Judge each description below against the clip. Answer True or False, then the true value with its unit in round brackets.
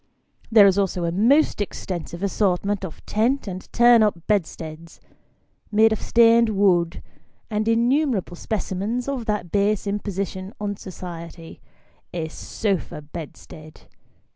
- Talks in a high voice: True (200 Hz)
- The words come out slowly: True (120 wpm)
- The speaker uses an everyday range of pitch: True (3.9 semitones)